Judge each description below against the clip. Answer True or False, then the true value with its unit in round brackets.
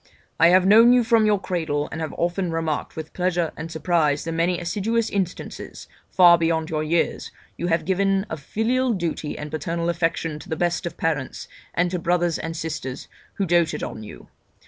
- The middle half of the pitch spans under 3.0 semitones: True (2.5 semitones)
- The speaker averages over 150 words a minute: True (190 wpm)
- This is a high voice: False (170 Hz)